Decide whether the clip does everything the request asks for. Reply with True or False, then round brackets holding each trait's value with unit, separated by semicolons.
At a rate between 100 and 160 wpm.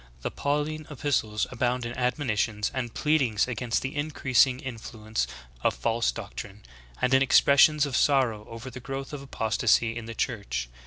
True (155 wpm)